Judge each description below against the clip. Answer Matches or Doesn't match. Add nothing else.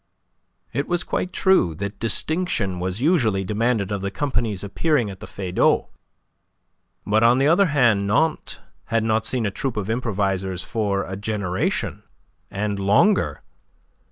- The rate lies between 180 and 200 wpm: Doesn't match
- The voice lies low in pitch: Matches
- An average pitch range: Matches